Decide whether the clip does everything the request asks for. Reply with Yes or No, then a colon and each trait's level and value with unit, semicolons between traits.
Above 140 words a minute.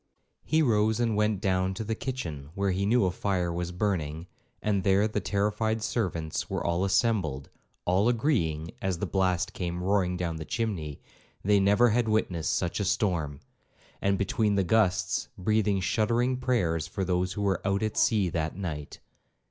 Yes: average, 170 wpm